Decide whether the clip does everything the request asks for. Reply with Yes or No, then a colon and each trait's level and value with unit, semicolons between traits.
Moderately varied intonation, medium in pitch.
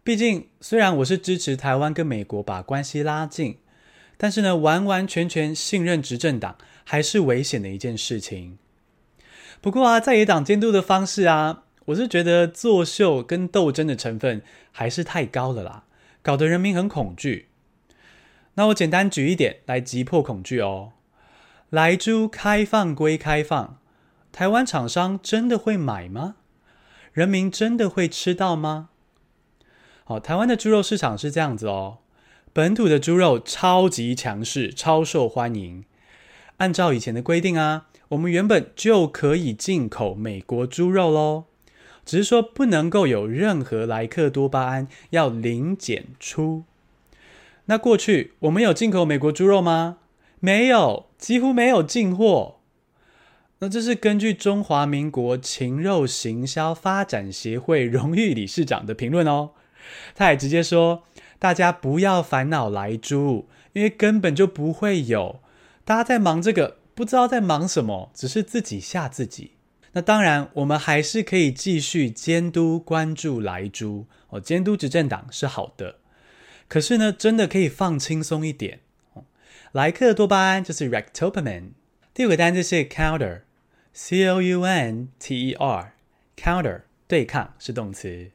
No: wide, 6.7 semitones; medium, 160 Hz